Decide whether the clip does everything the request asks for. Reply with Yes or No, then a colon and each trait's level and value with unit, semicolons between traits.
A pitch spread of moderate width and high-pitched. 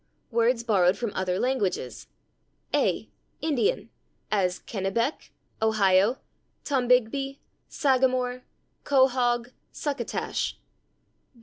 Yes: average, 4.1 semitones; high, 240 Hz